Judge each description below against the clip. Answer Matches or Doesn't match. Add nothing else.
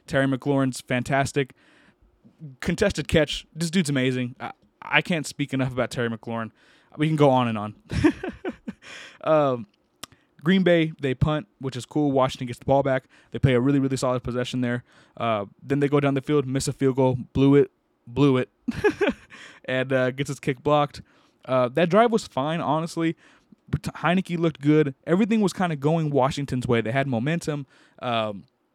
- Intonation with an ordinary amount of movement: Matches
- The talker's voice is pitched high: Doesn't match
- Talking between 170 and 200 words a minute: Matches